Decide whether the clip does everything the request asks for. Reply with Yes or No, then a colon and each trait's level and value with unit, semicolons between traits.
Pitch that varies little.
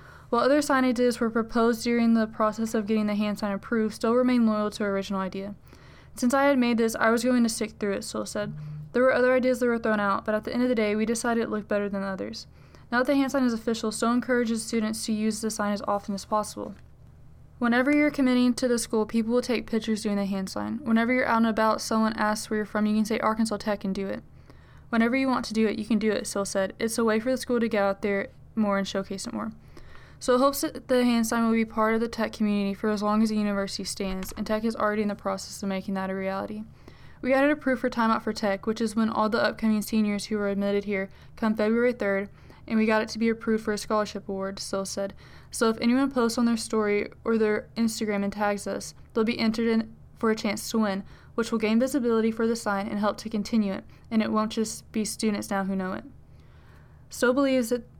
Yes: narrow, 2.2 semitones